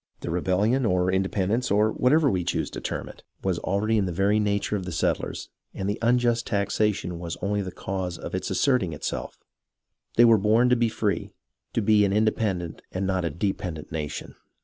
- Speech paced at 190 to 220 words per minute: Yes, average, 195 wpm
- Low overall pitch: Yes, low, 100 Hz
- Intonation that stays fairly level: No, average, 3.2 semitones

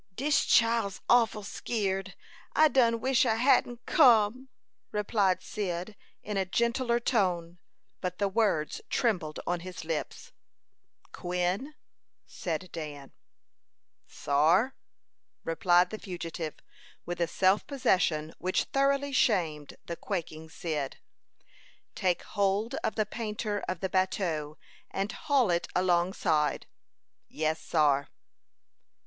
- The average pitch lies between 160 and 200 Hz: Yes, high, 190 Hz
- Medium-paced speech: No, slow, 110 wpm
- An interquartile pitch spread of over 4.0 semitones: Yes, average, 5.1 semitones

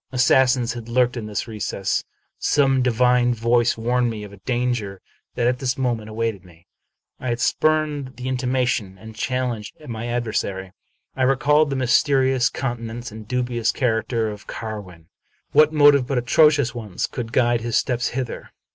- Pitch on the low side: Yes, low, 120 Hz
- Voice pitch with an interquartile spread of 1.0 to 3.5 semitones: Yes, narrow, 2.5 semitones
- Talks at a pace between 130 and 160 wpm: Yes, average, 155 wpm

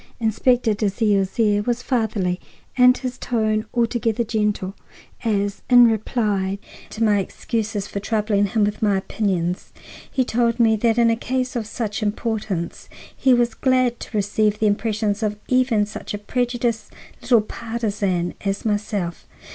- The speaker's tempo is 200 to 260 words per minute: No, average, 145 wpm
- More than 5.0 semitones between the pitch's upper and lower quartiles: No, narrow, 2.5 semitones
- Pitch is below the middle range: No, high, 220 Hz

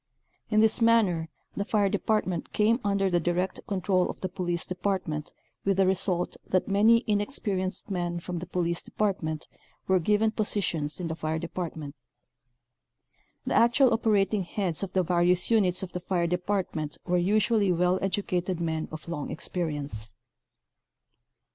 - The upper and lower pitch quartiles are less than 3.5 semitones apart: Yes, average, 2.9 semitones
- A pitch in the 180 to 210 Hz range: Yes, medium, 185 Hz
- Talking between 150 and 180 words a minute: Yes, average, 155 wpm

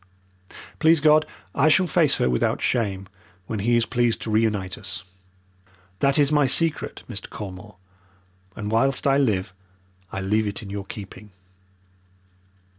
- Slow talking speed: No, average, 145 wpm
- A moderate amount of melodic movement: No, wide, 5.8 semitones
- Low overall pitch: Yes, low, 110 Hz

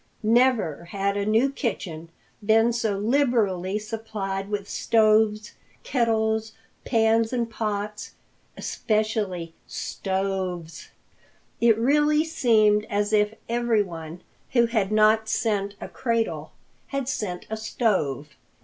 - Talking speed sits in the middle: No, slow, 105 wpm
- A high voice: Yes, high, 215 Hz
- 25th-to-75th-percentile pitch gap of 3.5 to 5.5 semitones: No, narrow, 2.6 semitones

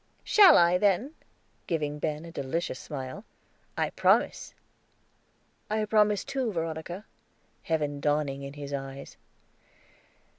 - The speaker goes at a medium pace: No, slow, 110 wpm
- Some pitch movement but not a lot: No, wide, 6.3 semitones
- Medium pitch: Yes, medium, 160 Hz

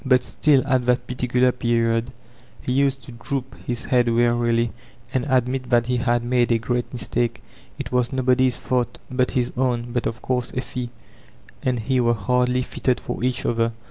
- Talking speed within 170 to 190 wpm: Yes, average, 180 wpm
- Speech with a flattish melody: Yes, narrow, 1.3 semitones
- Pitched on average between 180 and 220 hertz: No, low, 125 Hz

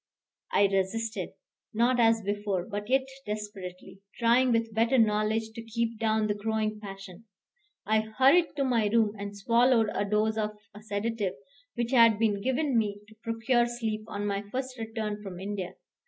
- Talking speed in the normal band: Yes, average, 165 wpm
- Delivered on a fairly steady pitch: Yes, narrow, 2.1 semitones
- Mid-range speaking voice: No, high, 220 Hz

